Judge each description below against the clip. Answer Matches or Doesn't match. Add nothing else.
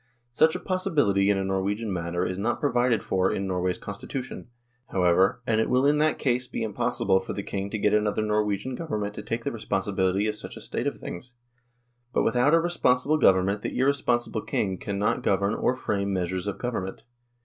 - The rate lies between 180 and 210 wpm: Matches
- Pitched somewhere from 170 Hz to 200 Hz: Doesn't match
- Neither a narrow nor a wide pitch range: Matches